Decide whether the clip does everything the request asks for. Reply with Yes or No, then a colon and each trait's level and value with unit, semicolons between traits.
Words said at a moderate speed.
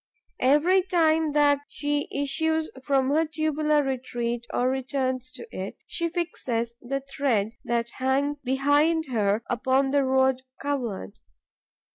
No: slow, 125 wpm